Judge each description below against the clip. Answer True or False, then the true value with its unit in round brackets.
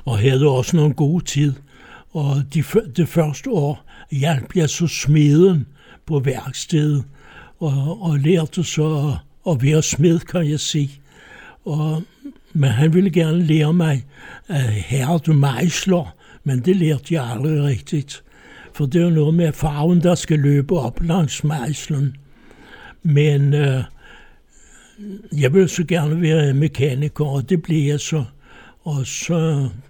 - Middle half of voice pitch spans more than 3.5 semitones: False (3.1 semitones)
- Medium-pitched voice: True (150 Hz)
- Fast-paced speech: False (145 wpm)